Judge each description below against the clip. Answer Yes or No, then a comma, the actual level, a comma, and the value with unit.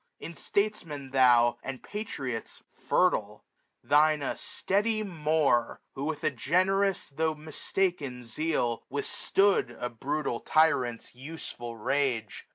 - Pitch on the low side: No, medium, 145 Hz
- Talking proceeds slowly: Yes, slow, 110 wpm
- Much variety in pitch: No, average, 4.9 semitones